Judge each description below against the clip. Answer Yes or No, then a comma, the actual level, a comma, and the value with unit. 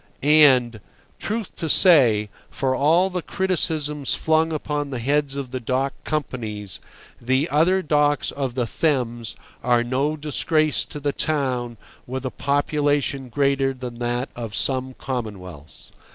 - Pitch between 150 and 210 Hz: No, low, 135 Hz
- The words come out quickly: No, average, 140 wpm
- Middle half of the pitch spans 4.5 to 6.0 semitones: No, average, 3.4 semitones